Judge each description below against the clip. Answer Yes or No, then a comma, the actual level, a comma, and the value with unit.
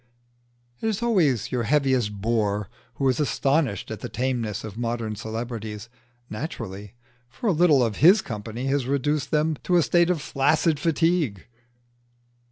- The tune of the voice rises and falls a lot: Yes, wide, 5.9 semitones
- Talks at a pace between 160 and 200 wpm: No, average, 150 wpm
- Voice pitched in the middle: No, low, 130 Hz